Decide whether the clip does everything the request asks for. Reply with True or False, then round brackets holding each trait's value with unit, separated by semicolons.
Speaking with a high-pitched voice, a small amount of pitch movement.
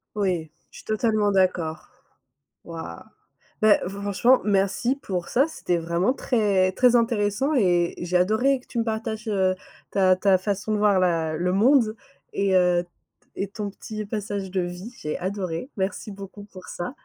False (200 Hz; 3.1 semitones)